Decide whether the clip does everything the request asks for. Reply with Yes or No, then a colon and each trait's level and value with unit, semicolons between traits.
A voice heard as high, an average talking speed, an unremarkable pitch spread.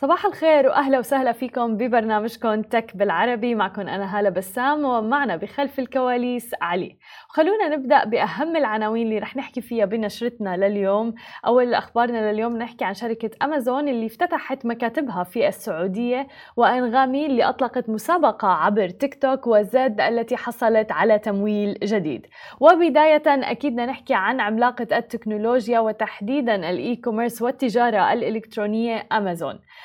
Yes: high, 235 Hz; average, 125 wpm; average, 3.7 semitones